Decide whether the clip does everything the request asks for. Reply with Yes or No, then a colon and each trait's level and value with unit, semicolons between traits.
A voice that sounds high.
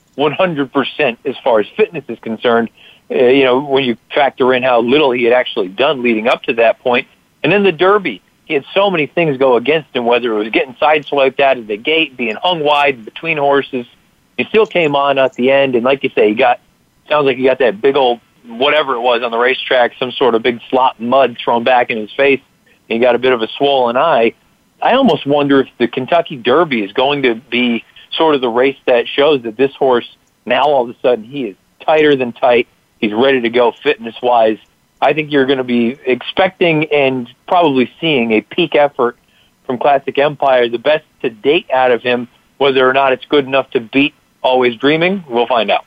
No: low, 135 Hz